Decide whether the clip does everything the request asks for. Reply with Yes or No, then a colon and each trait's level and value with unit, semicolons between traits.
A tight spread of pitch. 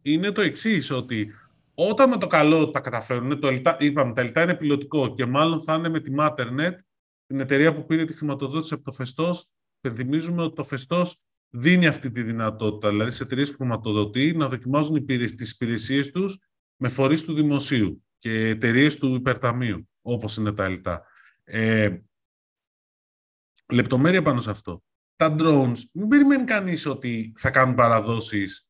No: average, 5.3 semitones